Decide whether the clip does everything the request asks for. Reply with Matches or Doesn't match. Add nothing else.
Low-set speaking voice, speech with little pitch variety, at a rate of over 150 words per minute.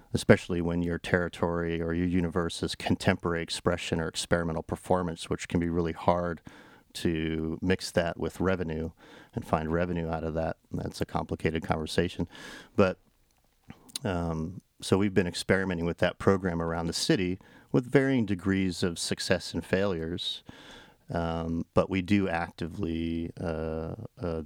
Doesn't match